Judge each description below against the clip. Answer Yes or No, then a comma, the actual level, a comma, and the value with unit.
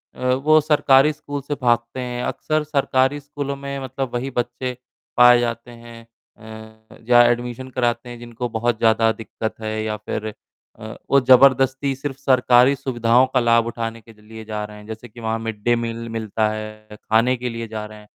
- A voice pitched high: No, low, 120 Hz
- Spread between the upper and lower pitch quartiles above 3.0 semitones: No, average, 2.7 semitones